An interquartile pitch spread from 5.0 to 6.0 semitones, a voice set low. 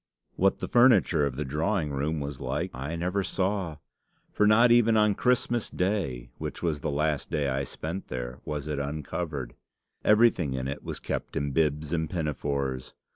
Yes: wide, 5.6 semitones; very low, 75 Hz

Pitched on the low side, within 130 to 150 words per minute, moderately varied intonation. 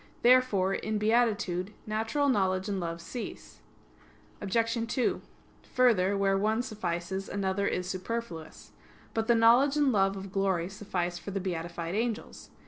No: high, 200 Hz; slow, 135 wpm; average, 3.6 semitones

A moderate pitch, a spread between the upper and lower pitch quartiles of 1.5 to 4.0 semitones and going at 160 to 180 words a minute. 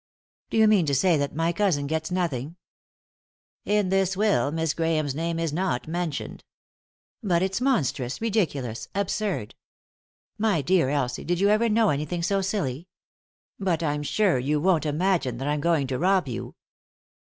No: medium, 165 Hz; average, 5.0 semitones; average, 170 wpm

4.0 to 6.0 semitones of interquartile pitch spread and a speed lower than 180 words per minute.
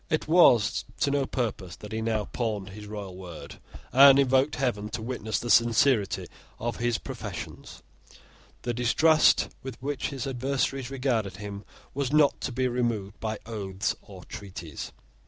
Yes: average, 4.4 semitones; average, 155 wpm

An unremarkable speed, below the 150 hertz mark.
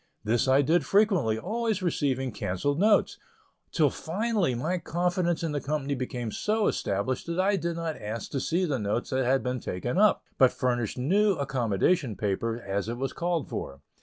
Yes: average, 180 wpm; medium, 140 Hz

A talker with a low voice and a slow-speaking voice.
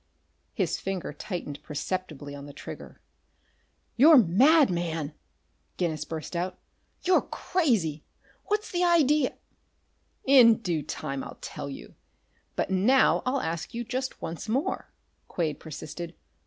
No: medium, 185 Hz; slow, 130 wpm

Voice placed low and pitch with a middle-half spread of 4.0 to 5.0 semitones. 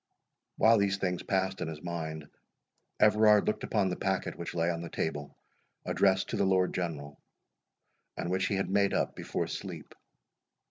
No: very low, 95 Hz; average, 2.9 semitones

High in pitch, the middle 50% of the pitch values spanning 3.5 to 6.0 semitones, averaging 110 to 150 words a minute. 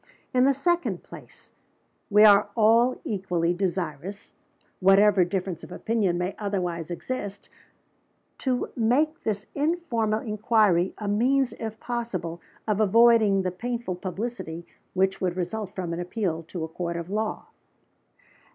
Yes: high, 205 Hz; average, 4.2 semitones; slow, 135 wpm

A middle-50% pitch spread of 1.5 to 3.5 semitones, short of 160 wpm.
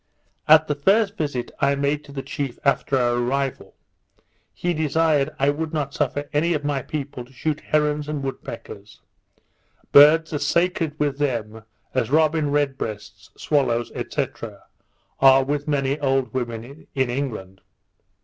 Yes: narrow, 2.4 semitones; average, 150 wpm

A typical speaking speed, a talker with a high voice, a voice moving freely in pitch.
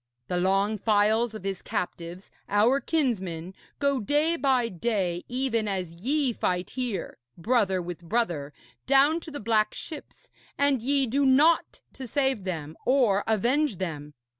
Yes: average, 145 wpm; high, 220 Hz; wide, 6.4 semitones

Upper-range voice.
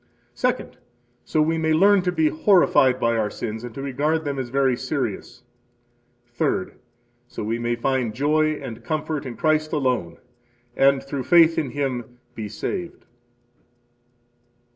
No: low, 135 Hz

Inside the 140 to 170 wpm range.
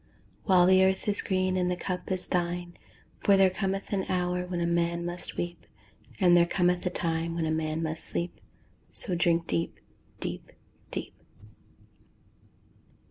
Yes: average, 160 wpm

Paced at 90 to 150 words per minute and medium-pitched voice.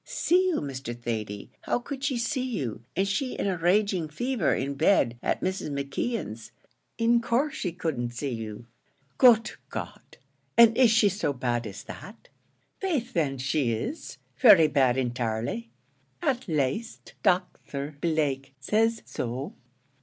Yes: average, 145 wpm; medium, 160 Hz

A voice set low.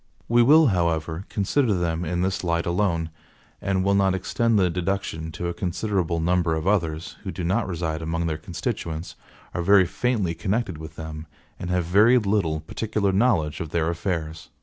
Yes: very low, 90 Hz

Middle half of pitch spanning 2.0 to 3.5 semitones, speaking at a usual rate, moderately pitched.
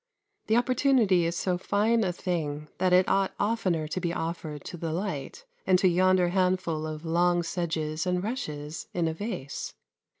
Yes: average, 2.8 semitones; average, 170 wpm; medium, 175 Hz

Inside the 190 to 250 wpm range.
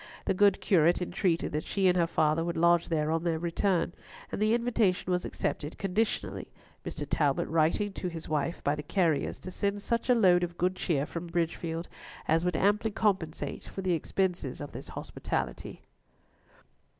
No: average, 175 wpm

